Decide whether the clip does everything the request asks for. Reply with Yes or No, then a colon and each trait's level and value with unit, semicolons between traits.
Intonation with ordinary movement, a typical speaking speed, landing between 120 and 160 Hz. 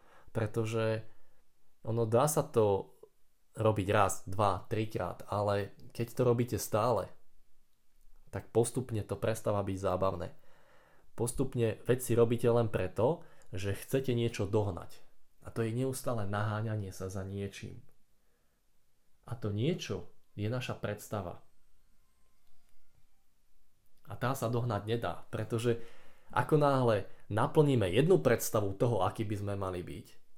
No: average, 3.2 semitones; average, 120 wpm; low, 110 Hz